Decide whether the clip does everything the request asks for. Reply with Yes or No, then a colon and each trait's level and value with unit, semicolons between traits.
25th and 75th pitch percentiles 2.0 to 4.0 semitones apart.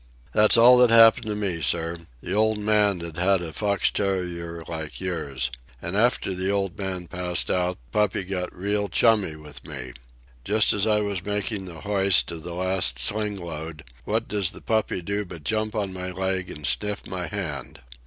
Yes: average, 3.4 semitones